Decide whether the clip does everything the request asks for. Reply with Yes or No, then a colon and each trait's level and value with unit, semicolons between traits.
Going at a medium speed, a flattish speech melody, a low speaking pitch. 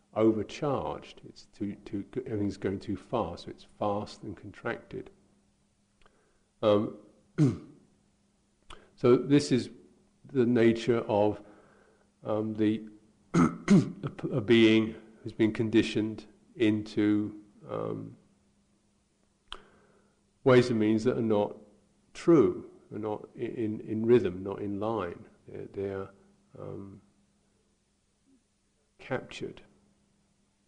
No: slow, 95 wpm; narrow, 2.3 semitones; low, 110 Hz